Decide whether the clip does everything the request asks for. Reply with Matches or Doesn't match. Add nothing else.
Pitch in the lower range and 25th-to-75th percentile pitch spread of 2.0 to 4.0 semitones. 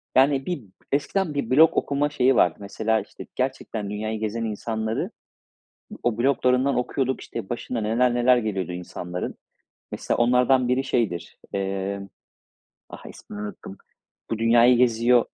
Matches